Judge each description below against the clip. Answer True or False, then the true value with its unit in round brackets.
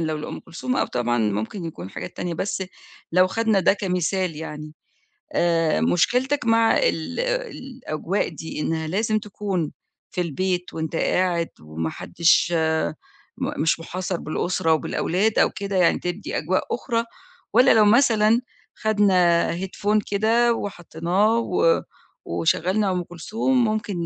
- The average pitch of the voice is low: False (185 Hz)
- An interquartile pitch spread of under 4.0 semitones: False (4.8 semitones)